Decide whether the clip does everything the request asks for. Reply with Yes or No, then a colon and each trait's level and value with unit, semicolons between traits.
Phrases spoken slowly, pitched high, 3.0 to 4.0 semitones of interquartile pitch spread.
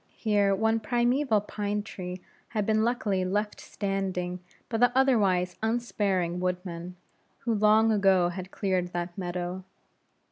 Yes: slow, 130 wpm; high, 200 Hz; average, 3.4 semitones